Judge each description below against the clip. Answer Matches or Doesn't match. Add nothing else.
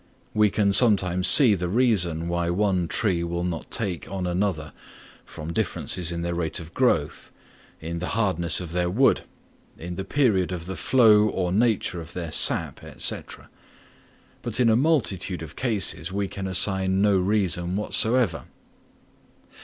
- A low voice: Matches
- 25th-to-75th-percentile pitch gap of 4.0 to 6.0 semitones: Doesn't match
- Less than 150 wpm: Doesn't match